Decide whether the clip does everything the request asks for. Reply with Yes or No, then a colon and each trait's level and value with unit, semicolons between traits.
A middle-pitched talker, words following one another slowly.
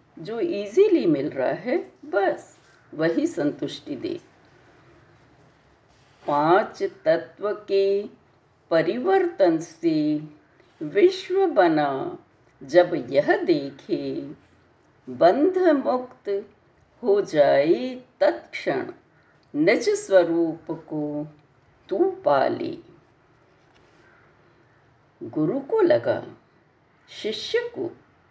No: very high, 300 Hz; slow, 70 wpm